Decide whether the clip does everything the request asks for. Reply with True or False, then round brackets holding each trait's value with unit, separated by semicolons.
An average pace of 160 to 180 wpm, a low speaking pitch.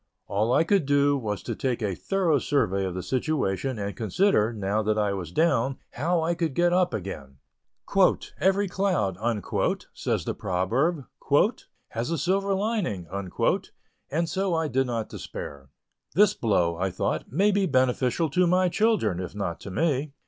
True (165 wpm; 130 Hz)